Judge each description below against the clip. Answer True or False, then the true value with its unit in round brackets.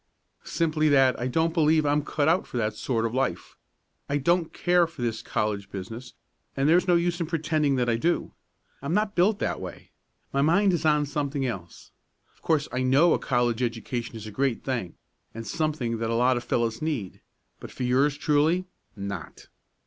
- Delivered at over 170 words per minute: True (185 wpm)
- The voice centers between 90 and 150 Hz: True (140 Hz)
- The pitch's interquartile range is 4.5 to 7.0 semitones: True (5.3 semitones)